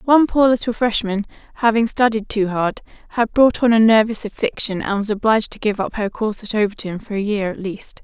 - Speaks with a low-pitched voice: No, high, 215 Hz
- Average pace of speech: No, fast, 215 wpm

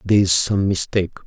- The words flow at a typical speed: Yes, average, 190 wpm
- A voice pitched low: Yes, very low, 95 Hz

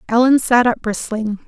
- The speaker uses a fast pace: No, average, 160 wpm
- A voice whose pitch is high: Yes, high, 230 Hz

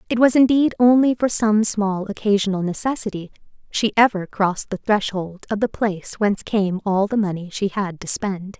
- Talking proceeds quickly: No, average, 180 wpm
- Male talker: No, female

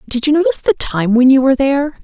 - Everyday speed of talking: No, fast, 265 wpm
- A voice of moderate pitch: No, very high, 275 Hz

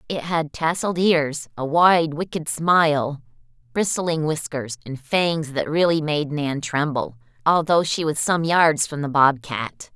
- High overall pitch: No, medium, 150 Hz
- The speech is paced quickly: No, average, 150 wpm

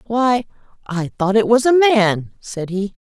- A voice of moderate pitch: No, high, 215 Hz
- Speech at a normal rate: Yes, average, 180 wpm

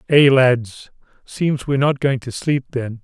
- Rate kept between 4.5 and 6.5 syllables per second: No, 4.1 syllables/s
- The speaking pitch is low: Yes, low, 130 Hz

